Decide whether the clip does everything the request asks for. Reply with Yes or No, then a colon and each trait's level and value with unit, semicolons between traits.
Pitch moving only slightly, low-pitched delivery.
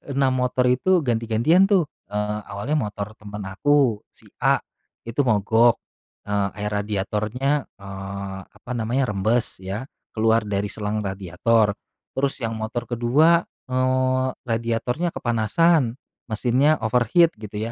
No: average, 3.8 semitones; low, 115 Hz